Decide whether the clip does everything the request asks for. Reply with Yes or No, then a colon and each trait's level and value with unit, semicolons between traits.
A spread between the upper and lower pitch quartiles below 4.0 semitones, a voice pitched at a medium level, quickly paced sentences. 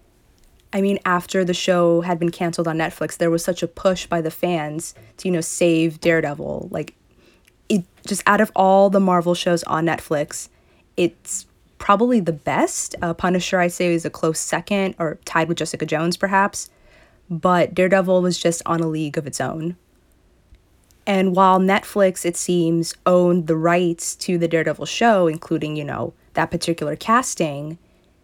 No: narrow, 2.5 semitones; medium, 170 Hz; average, 170 wpm